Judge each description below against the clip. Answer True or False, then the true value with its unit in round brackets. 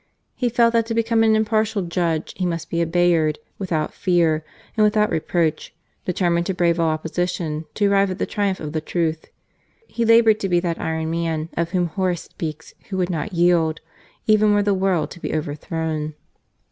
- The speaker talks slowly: False (195 wpm)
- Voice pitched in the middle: True (175 Hz)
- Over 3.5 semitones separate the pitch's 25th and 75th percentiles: True (3.9 semitones)